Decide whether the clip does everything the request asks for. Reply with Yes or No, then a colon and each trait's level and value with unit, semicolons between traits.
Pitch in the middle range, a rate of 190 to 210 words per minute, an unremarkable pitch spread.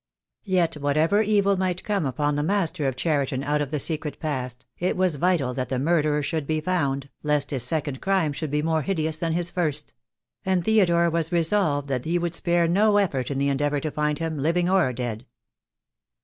Yes: medium, 155 Hz; fast, 205 wpm; average, 3.5 semitones